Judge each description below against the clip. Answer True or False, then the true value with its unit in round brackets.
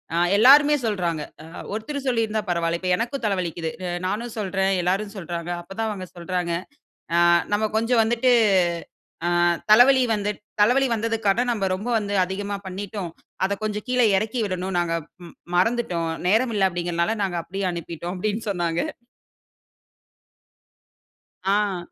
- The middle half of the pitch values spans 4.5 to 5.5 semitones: False (4.0 semitones)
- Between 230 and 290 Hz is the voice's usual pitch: False (200 Hz)